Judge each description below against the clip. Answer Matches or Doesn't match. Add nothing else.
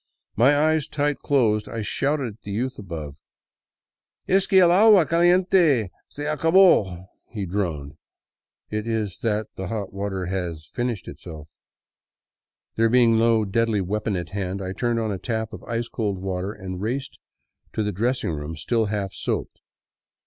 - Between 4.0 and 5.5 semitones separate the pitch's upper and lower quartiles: Matches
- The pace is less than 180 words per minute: Matches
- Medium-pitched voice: Doesn't match